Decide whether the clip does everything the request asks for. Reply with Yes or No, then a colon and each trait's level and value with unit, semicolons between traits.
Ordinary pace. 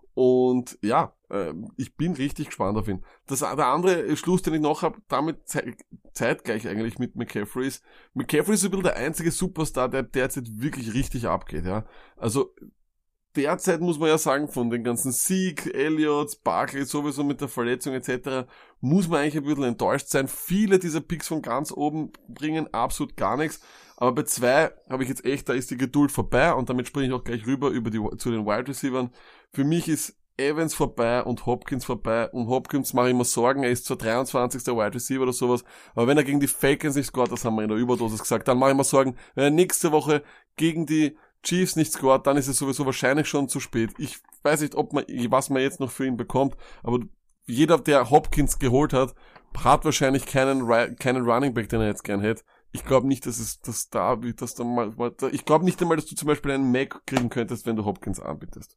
No: fast, 215 wpm